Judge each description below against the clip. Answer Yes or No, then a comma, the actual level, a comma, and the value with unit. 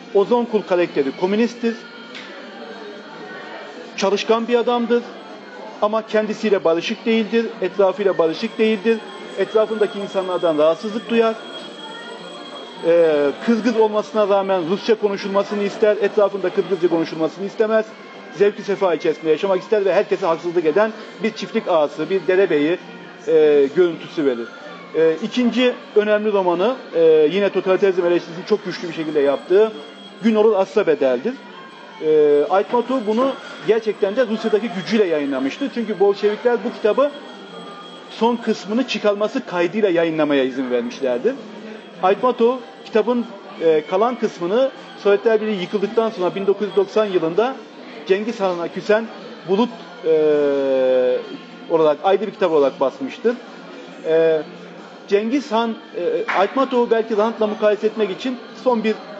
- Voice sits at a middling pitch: No, high, 210 Hz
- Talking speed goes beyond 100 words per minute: Yes, average, 120 wpm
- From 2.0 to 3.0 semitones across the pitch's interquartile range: No, average, 3.8 semitones